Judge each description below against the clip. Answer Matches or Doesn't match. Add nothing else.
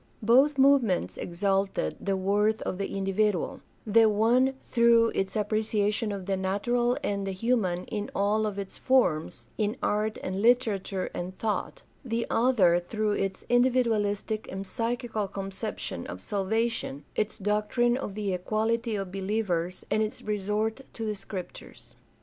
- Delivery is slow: Doesn't match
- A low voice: Doesn't match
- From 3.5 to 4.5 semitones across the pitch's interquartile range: Doesn't match